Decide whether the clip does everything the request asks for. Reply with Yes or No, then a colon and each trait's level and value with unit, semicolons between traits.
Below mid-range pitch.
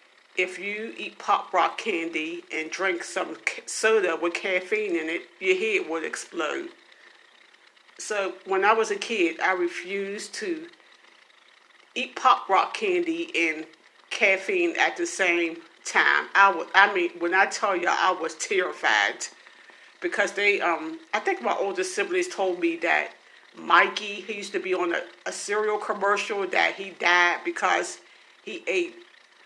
No: high, 220 Hz